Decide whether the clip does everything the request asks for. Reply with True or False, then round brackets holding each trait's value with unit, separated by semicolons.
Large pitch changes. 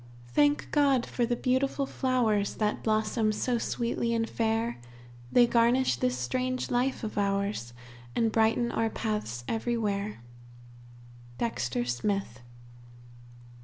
False (3.1 semitones)